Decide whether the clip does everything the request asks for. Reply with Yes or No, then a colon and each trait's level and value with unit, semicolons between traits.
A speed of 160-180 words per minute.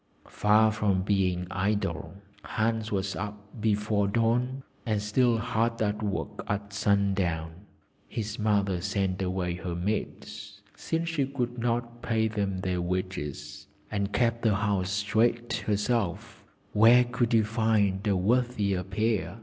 No: slow, 135 wpm